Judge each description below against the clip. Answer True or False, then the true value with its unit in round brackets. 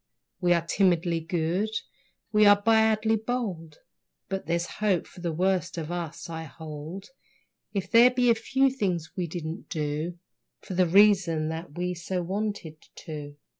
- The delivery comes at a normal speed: True (155 wpm)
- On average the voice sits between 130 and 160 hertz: False (180 Hz)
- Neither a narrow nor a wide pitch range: True (3.9 semitones)